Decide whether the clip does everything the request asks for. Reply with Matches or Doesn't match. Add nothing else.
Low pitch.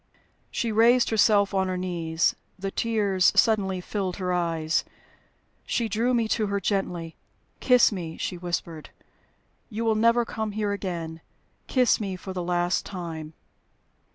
Doesn't match